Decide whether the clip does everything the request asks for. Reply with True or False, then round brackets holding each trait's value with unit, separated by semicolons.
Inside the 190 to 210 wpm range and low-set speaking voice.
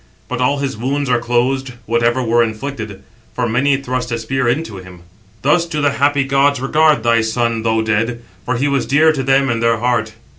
True (200 wpm; 125 Hz)